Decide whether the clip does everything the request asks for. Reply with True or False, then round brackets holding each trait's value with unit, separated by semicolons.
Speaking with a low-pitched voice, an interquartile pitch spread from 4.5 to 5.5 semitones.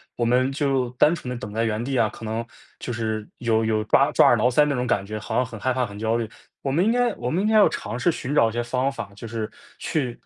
False (120 Hz; 3.3 semitones)